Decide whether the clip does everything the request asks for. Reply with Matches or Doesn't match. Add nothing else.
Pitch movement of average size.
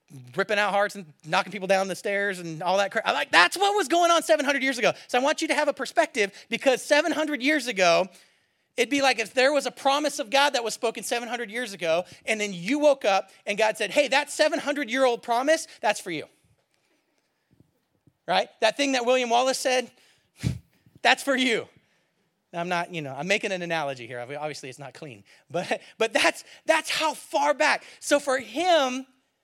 Doesn't match